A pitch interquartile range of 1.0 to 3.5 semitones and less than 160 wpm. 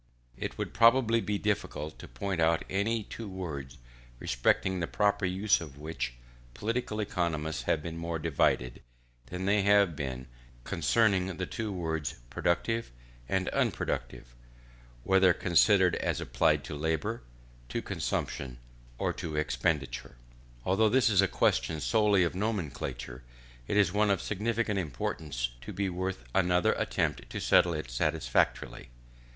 No: average, 5.1 semitones; average, 140 wpm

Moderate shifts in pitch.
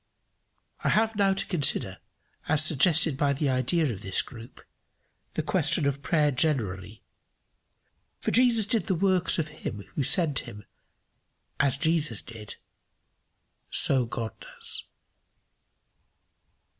No: wide, 6.1 semitones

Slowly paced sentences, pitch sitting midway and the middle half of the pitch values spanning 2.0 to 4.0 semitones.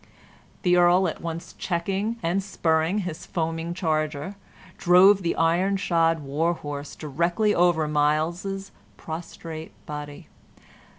Yes: slow, 115 wpm; medium, 170 Hz; narrow, 2.6 semitones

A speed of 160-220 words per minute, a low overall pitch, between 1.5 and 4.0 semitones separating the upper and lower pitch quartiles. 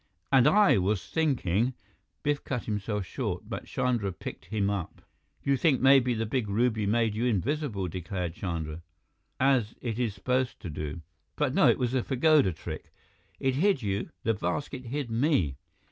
No: average, 170 wpm; low, 115 Hz; average, 5.2 semitones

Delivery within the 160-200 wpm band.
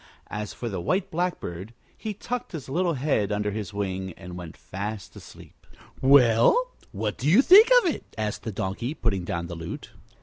Yes: average, 180 wpm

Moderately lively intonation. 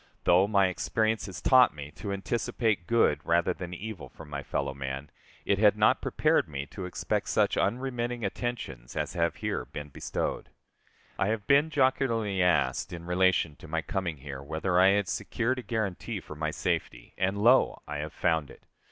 No: wide, 6.1 semitones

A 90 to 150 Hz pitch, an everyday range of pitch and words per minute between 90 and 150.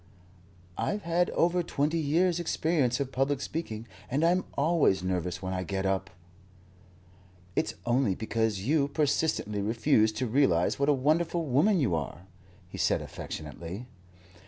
No: low, 135 Hz; wide, 7.9 semitones; average, 140 wpm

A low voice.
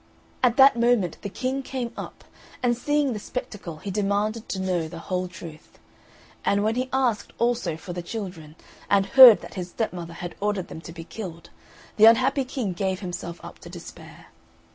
No: high, 200 Hz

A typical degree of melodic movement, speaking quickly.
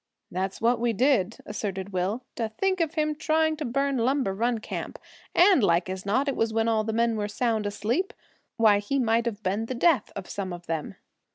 Yes: average, 4.7 semitones; fast, 215 wpm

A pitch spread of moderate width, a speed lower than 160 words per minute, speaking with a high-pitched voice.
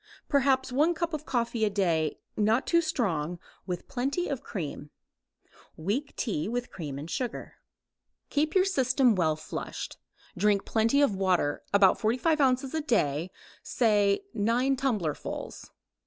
No: wide, 6.5 semitones; average, 140 wpm; high, 230 Hz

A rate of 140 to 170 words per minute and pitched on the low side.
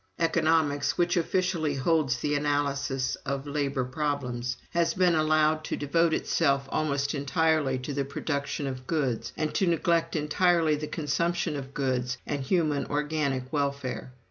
No: average, 145 wpm; medium, 145 Hz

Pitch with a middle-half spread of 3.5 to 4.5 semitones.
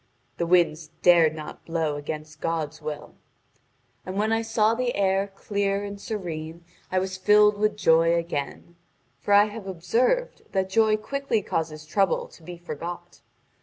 Yes: average, 4.2 semitones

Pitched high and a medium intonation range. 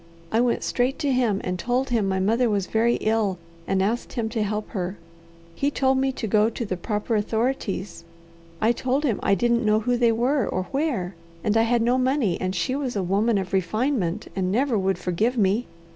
Yes: high, 225 Hz; average, 4.1 semitones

